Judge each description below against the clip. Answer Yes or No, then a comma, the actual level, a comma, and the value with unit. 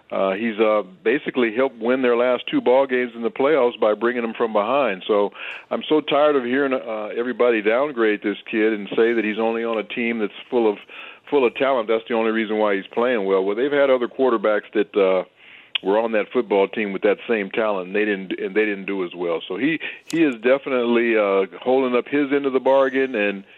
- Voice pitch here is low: Yes, low, 115 Hz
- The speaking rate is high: Yes, fast, 230 wpm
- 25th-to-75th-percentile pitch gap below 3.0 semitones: No, average, 3.7 semitones